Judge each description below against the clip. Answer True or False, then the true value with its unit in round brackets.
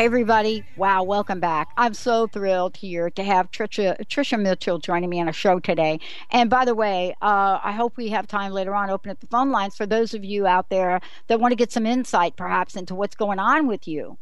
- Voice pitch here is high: True (200 Hz)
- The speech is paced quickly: True (230 wpm)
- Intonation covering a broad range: False (3.9 semitones)